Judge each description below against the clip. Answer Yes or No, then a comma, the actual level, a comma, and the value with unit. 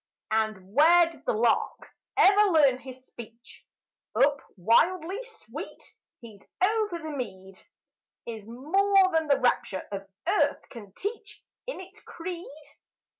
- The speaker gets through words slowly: Yes, slow, 125 wpm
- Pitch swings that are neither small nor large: No, wide, 8.7 semitones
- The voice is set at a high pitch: Yes, very high, 295 Hz